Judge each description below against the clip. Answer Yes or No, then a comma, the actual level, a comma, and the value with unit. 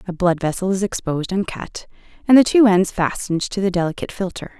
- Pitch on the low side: No, high, 190 Hz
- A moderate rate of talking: No, fast, 210 wpm